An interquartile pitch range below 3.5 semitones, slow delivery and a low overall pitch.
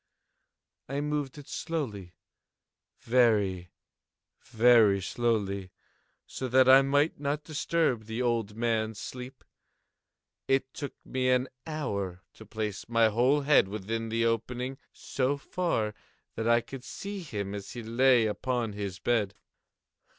No: average, 3.8 semitones; slow, 125 wpm; low, 120 Hz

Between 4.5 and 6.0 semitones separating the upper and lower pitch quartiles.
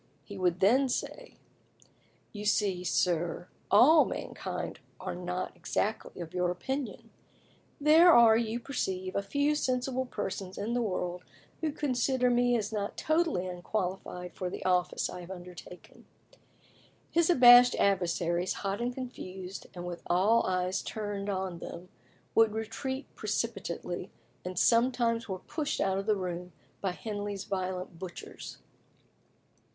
Yes: average, 5.0 semitones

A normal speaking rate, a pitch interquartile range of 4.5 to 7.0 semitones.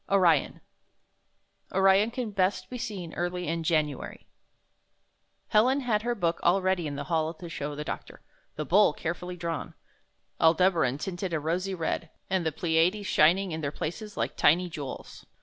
No: average, 160 wpm; average, 3.3 semitones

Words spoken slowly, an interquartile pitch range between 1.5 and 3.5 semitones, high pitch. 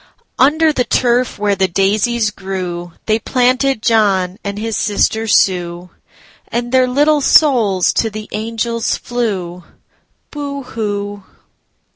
No: slow, 105 wpm; average, 4.2 semitones; high, 220 Hz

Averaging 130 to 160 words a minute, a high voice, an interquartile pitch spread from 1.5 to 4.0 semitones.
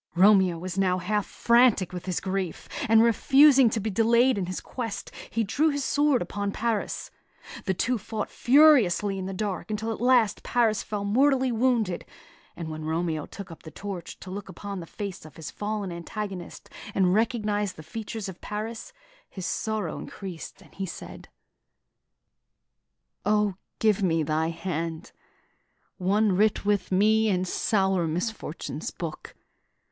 Yes: average, 155 wpm; high, 205 Hz; average, 3.5 semitones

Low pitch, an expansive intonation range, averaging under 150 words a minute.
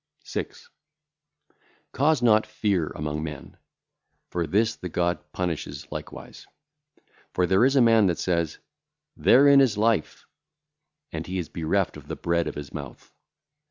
Yes: very low, 90 Hz; wide, 5.9 semitones; average, 140 wpm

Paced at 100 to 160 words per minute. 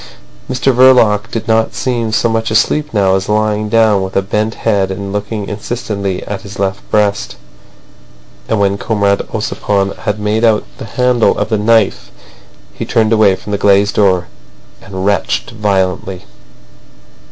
Yes: average, 155 wpm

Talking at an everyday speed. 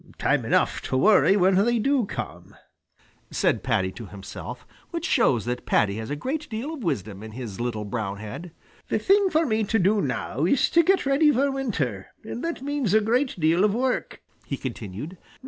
Yes: average, 195 wpm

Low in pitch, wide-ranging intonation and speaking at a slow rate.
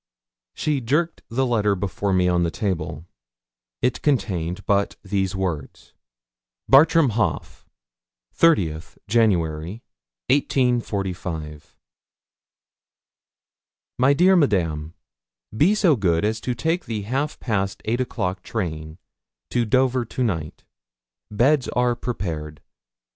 Yes: low, 105 Hz; wide, 6.6 semitones; slow, 105 wpm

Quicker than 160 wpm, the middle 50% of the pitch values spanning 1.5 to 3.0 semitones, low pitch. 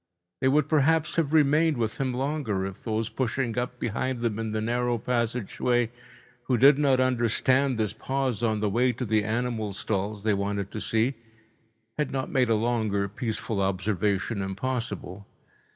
No: average, 170 wpm; average, 3.5 semitones; low, 115 Hz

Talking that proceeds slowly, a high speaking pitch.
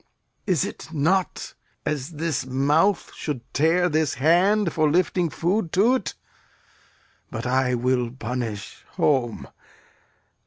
No: slow, 110 wpm; medium, 155 Hz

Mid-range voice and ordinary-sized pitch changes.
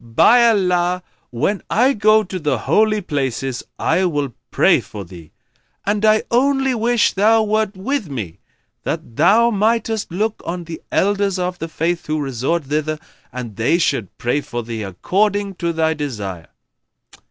No: medium, 175 Hz; wide, 7.8 semitones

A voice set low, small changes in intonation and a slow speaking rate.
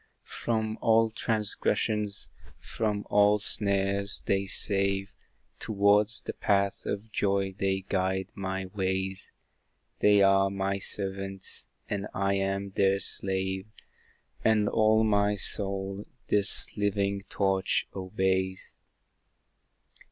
Yes: low, 100 Hz; narrow, 1.1 semitones; slow, 100 wpm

